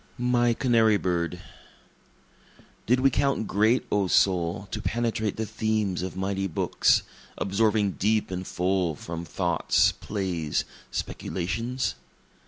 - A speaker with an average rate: No, slow, 115 wpm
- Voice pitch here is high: No, low, 100 Hz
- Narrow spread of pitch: No, average, 3.4 semitones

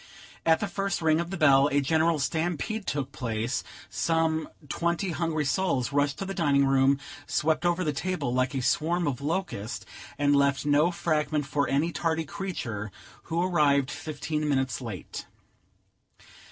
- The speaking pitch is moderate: Yes, medium, 150 Hz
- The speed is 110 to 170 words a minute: Yes, average, 155 wpm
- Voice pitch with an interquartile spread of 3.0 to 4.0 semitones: Yes, average, 3.5 semitones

